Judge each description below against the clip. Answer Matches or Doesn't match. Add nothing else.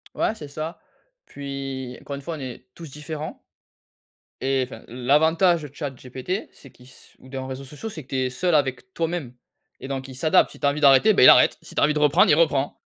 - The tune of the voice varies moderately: Matches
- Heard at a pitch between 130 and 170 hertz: Matches